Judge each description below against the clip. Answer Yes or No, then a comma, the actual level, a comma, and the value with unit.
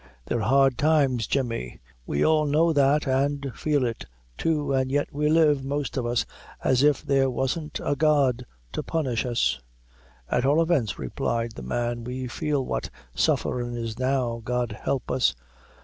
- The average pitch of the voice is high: No, low, 135 Hz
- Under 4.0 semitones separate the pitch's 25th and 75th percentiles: Yes, average, 3.3 semitones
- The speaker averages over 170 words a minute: No, average, 165 wpm